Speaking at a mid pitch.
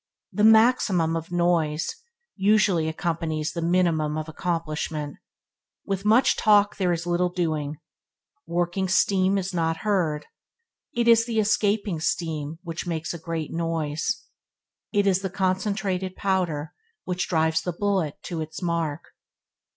Yes: medium, 175 Hz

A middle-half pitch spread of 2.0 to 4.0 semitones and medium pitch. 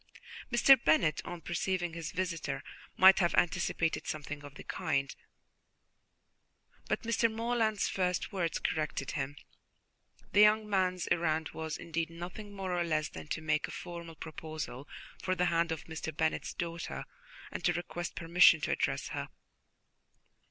Yes: average, 2.9 semitones; medium, 170 Hz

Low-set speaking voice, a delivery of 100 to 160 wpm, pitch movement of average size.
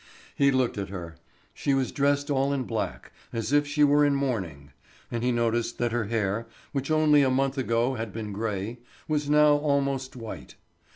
No: low, 130 Hz; average, 185 wpm; average, 3.9 semitones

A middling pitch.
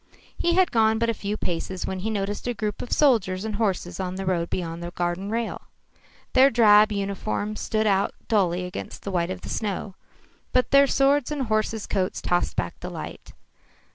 No: high, 205 Hz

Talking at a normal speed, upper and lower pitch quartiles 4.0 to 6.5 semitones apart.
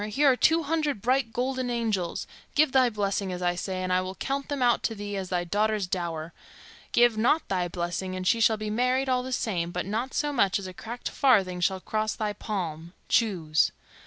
No: fast, 215 wpm; average, 5.3 semitones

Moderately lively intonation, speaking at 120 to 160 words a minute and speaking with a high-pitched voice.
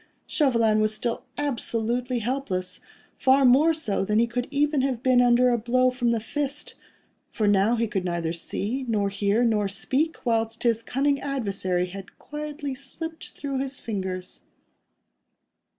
Yes: average, 4.3 semitones; average, 150 wpm; high, 240 Hz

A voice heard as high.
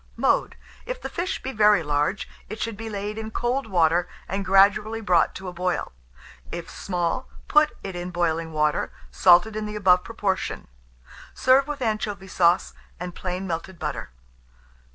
Yes: high, 195 Hz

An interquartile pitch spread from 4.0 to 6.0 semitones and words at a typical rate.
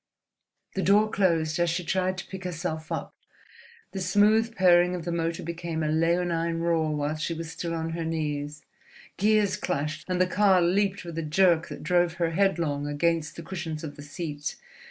No: narrow, 2.4 semitones; average, 185 wpm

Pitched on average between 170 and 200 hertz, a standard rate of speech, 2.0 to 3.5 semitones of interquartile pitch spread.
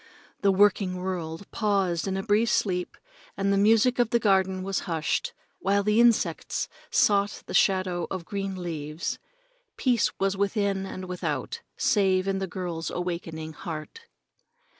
Yes: high, 190 Hz; average, 145 wpm; narrow, 2.4 semitones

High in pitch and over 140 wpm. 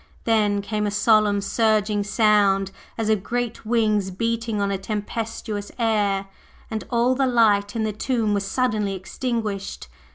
Yes: high, 215 Hz; average, 150 wpm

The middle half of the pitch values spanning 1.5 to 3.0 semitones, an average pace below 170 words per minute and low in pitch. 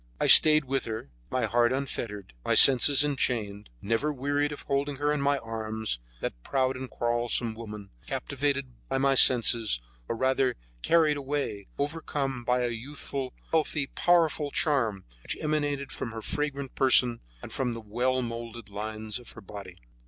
No: average, 3.9 semitones; average, 160 wpm; low, 130 Hz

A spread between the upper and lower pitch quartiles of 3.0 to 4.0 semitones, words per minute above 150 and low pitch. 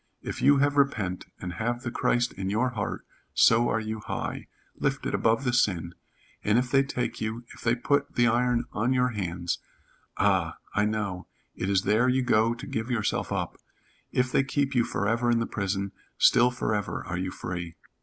Yes: average, 3.7 semitones; average, 190 wpm; low, 115 Hz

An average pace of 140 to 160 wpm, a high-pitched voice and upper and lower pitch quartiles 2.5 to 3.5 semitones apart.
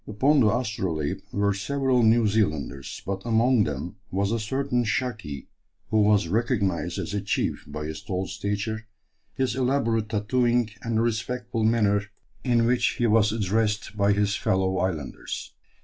No: average, 150 wpm; low, 105 Hz; average, 3.0 semitones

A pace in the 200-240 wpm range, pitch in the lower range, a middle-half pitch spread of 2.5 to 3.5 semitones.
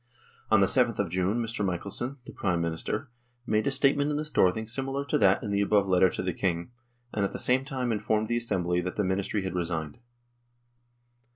No: fast, 205 wpm; low, 105 Hz; average, 4.7 semitones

